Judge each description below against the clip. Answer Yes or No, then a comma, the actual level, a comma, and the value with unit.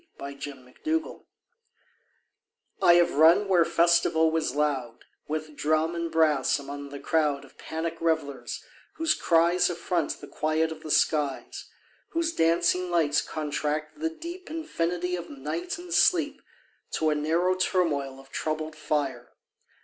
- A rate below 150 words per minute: Yes, average, 140 wpm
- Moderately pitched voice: Yes, medium, 160 Hz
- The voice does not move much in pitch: No, average, 3.0 semitones